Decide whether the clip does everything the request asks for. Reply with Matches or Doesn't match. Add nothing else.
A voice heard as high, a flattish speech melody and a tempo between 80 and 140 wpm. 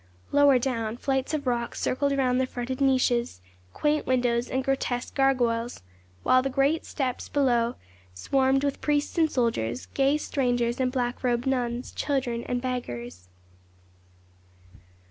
Matches